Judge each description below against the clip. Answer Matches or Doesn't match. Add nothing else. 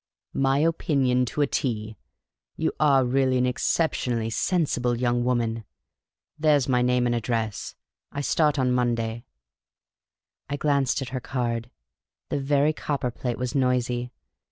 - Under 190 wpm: Matches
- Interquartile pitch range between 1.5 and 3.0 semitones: Matches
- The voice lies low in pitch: Matches